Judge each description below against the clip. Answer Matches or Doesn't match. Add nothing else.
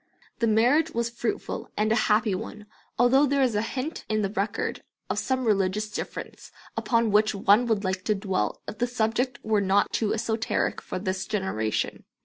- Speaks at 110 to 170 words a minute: Doesn't match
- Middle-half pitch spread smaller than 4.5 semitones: Matches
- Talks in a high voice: Matches